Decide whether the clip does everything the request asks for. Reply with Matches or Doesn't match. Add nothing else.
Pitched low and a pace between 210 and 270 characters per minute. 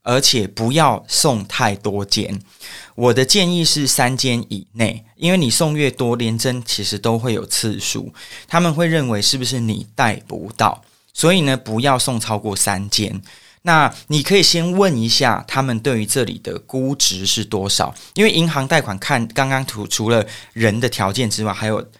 Matches